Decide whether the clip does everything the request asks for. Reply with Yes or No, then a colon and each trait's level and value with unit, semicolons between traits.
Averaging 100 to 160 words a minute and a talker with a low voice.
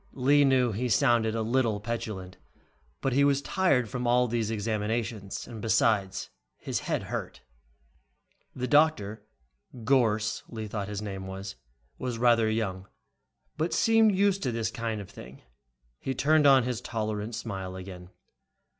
Yes: average, 145 wpm; low, 115 Hz